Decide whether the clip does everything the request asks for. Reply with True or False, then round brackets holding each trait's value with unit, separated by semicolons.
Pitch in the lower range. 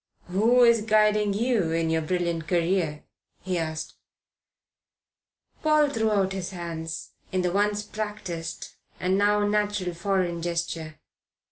False (190 Hz)